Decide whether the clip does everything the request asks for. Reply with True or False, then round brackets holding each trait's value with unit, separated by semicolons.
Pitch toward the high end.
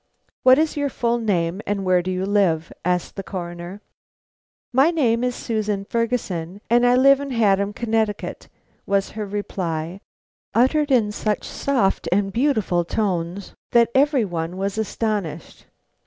True (205 Hz)